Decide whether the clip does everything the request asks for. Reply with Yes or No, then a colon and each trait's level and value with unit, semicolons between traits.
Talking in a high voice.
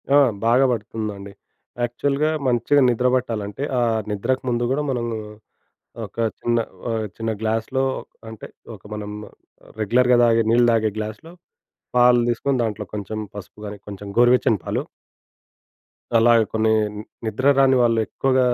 No: low, 115 Hz